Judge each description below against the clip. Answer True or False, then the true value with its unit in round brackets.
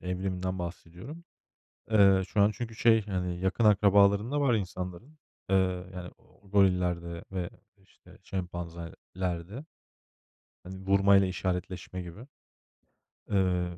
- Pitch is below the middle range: True (95 Hz)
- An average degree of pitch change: False (2.2 semitones)